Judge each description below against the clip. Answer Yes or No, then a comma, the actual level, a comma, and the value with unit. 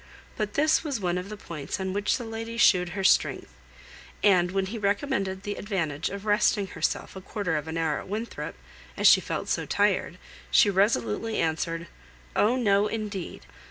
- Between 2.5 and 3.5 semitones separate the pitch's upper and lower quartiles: Yes, average, 3.1 semitones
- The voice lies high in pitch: Yes, high, 200 Hz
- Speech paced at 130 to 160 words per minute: No, average, 180 wpm